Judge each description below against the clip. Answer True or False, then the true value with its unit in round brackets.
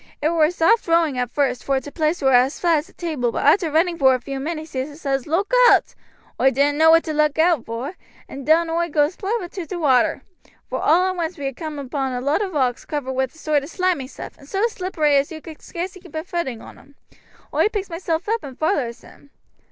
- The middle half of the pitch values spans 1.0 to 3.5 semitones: False (3.9 semitones)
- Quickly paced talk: True (245 wpm)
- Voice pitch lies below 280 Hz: False (310 Hz)